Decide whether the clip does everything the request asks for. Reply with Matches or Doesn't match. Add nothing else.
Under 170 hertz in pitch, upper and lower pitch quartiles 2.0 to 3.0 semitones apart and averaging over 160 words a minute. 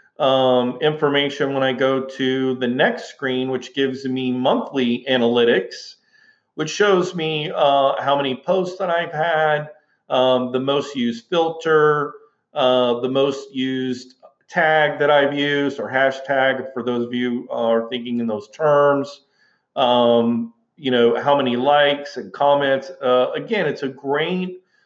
Doesn't match